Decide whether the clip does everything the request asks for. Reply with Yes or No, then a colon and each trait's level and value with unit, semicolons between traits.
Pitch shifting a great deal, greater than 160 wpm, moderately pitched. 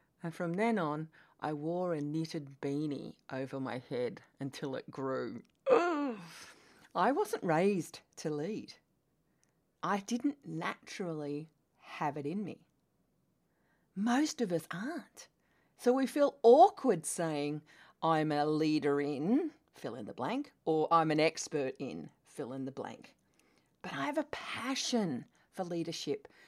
No: wide, 8.0 semitones; average, 140 wpm; medium, 170 Hz